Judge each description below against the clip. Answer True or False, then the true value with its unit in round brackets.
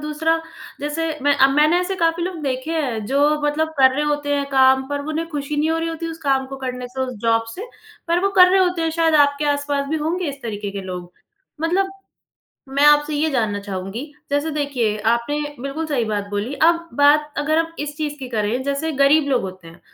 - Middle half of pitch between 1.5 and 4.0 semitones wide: True (3.5 semitones)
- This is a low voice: False (290 Hz)